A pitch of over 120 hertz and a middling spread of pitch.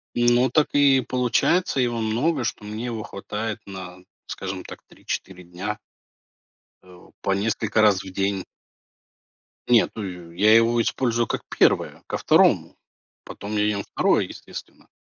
No: low, 110 Hz; average, 3.6 semitones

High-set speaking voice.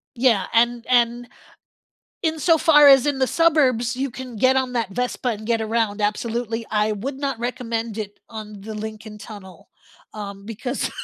Yes: high, 235 Hz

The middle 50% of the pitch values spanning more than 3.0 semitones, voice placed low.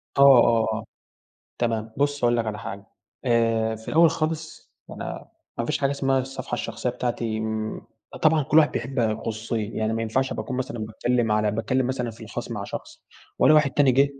Yes: average, 3.4 semitones; low, 120 Hz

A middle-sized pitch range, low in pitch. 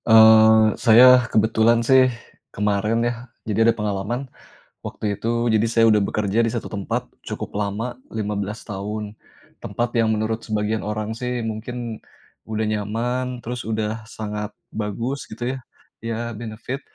No: narrow, 1.9 semitones; low, 110 Hz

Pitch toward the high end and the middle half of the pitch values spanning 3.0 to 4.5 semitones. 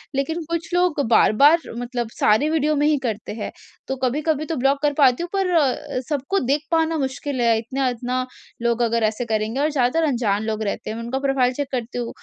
Yes: very high, 265 Hz; average, 4.2 semitones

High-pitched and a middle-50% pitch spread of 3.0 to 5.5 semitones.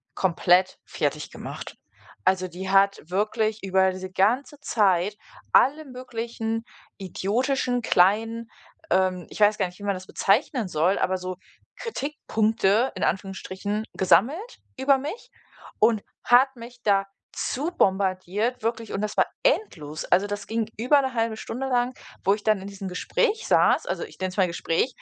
Yes: high, 210 Hz; average, 4.5 semitones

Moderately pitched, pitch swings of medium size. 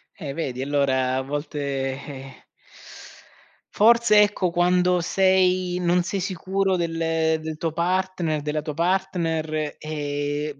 Yes: medium, 165 Hz; average, 3.8 semitones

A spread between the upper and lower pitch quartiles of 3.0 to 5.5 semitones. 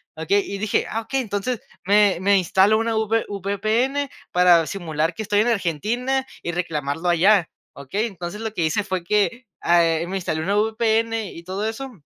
Yes: average, 4.2 semitones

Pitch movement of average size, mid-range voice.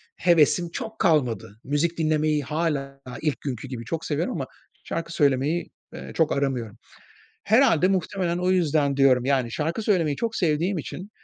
Yes: average, 3.9 semitones; medium, 155 Hz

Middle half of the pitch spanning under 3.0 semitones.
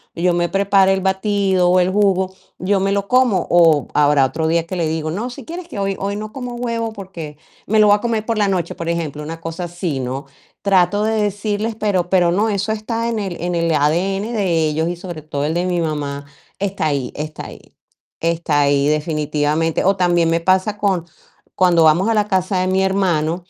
No: average, 3.8 semitones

